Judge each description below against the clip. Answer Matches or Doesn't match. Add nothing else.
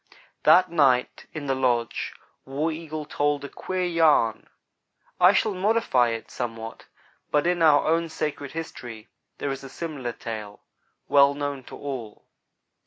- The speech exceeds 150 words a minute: Doesn't match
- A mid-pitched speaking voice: Matches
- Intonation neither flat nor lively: Matches